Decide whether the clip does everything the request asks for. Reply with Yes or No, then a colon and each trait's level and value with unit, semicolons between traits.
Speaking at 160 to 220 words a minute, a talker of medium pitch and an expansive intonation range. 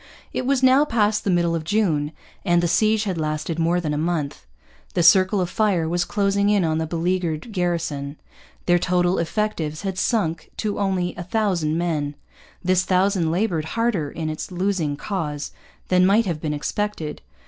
No: average, 175 wpm; medium, 175 Hz; average, 4.0 semitones